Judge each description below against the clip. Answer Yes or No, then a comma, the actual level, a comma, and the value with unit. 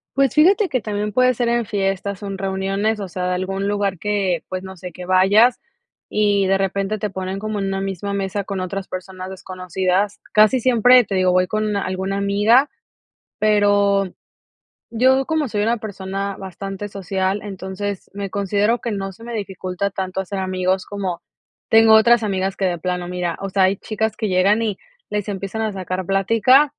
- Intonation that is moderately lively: No, narrow, 2.1 semitones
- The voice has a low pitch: No, high, 195 Hz